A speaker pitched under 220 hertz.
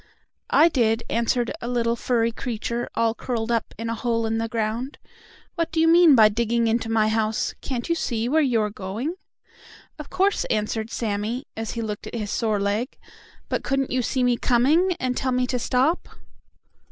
No: high, 235 Hz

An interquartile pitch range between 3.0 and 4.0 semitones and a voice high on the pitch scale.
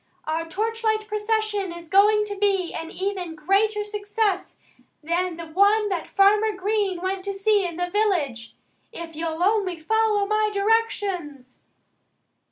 Yes: average, 3.7 semitones; very high, 395 Hz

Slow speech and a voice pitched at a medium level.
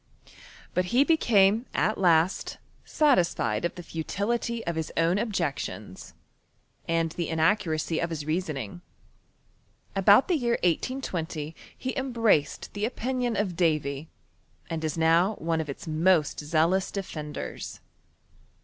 Yes: slow, 120 wpm; medium, 170 Hz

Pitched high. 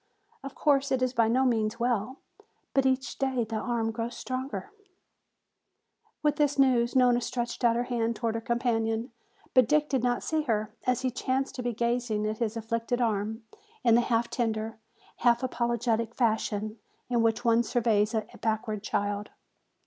Yes: high, 235 Hz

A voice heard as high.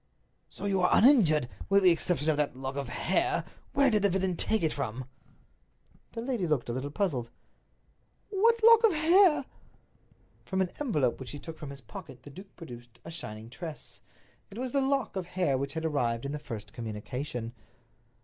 No: medium, 160 Hz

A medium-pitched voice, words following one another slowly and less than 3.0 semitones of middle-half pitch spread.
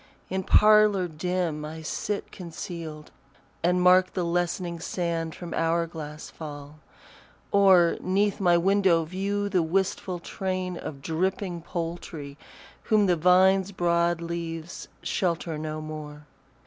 Yes: medium, 175 Hz; slow, 120 wpm; narrow, 2.4 semitones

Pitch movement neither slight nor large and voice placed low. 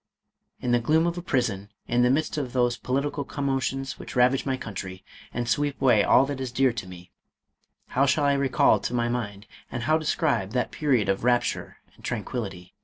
Yes: average, 3.2 semitones; low, 125 Hz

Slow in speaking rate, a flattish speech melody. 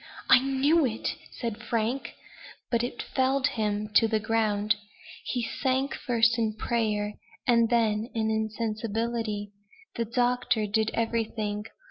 Yes: slow, 125 wpm; narrow, 2.0 semitones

